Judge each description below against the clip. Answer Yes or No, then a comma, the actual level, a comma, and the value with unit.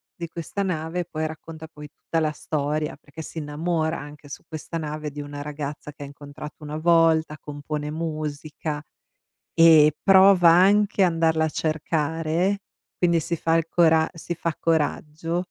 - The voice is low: No, medium, 160 Hz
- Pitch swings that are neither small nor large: No, narrow, 1.9 semitones